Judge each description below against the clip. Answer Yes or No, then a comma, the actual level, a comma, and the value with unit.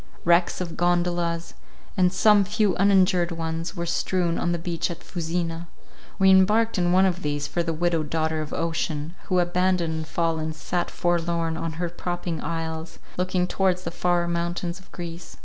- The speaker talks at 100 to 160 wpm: No, average, 170 wpm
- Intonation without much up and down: Yes, narrow, 1.6 semitones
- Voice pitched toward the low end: No, medium, 175 Hz